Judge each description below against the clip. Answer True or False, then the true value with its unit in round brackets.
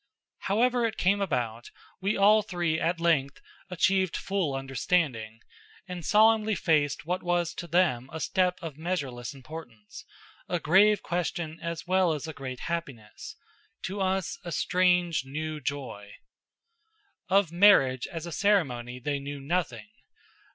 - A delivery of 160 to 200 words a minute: False (135 wpm)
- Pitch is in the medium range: True (170 Hz)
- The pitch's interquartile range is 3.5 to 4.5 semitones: False (5.0 semitones)